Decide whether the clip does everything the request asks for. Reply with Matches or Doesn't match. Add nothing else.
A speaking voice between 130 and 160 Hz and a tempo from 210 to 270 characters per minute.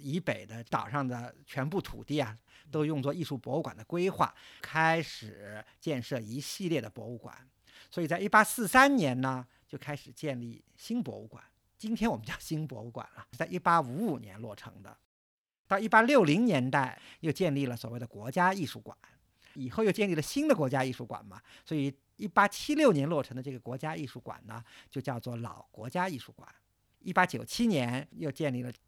Doesn't match